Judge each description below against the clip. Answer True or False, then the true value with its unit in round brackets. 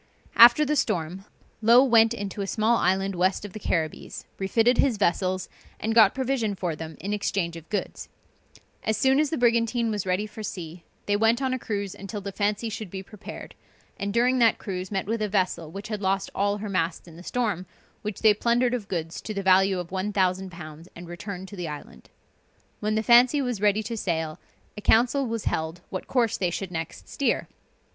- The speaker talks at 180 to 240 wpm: True (200 wpm)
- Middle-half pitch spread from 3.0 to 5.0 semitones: True (3.7 semitones)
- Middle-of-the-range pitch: False (205 Hz)